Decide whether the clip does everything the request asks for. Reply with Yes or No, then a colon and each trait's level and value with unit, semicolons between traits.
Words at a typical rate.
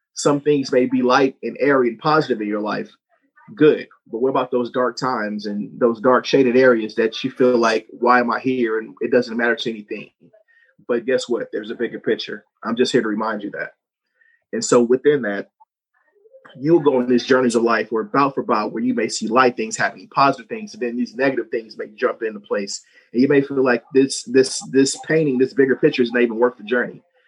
No: fast, 225 wpm